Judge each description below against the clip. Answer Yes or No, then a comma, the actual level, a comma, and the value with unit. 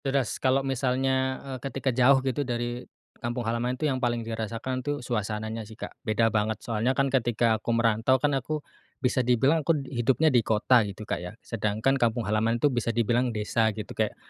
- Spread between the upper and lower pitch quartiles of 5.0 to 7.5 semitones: No, average, 2.8 semitones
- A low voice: Yes, low, 120 Hz